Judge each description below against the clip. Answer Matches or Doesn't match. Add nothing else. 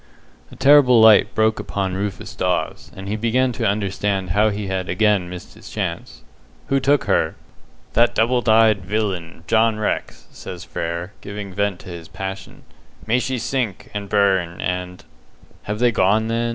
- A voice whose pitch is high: Doesn't match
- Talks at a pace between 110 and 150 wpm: Doesn't match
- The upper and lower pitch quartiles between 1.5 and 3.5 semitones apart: Matches